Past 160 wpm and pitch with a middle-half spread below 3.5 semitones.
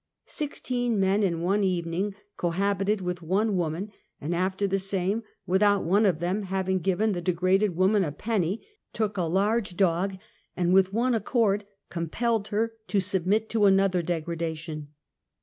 Yes: average, 170 wpm; average, 2.9 semitones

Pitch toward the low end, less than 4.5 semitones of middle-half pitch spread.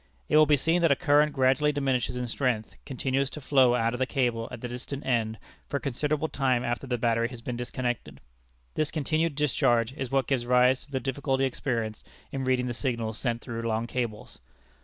Yes: low, 130 Hz; average, 2.7 semitones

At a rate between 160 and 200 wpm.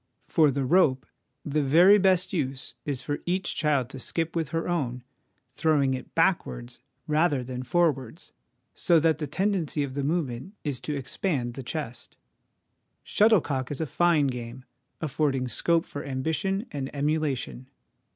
No: average, 150 wpm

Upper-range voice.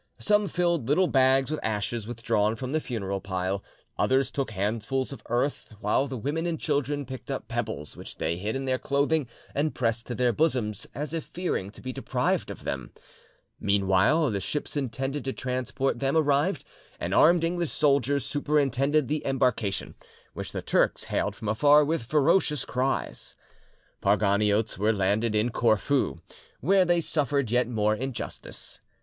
No: low, 130 Hz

